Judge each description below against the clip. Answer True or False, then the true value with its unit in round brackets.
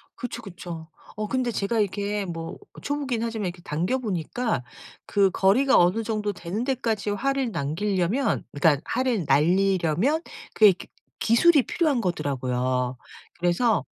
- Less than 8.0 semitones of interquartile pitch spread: True (5.6 semitones)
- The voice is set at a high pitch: True (205 Hz)